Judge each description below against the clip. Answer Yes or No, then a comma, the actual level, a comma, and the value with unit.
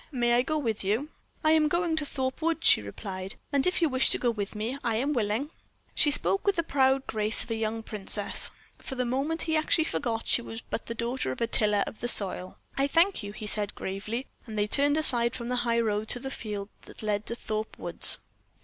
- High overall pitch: Yes, high, 235 Hz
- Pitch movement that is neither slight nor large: Yes, average, 4.8 semitones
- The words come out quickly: Yes, fast, 235 wpm